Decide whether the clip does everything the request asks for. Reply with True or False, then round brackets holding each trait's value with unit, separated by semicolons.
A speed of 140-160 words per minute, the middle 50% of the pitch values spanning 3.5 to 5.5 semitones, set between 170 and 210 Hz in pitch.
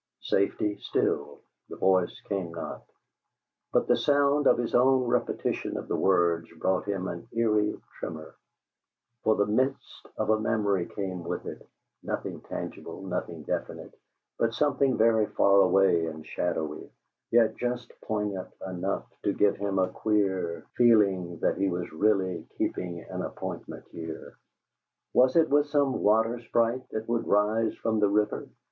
False (150 wpm; 3.9 semitones; 105 Hz)